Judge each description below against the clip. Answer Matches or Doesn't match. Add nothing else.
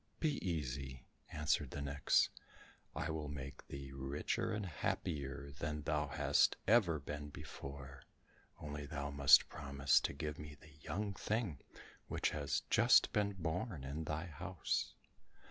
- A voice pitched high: Doesn't match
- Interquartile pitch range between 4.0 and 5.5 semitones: Doesn't match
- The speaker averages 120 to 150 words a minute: Matches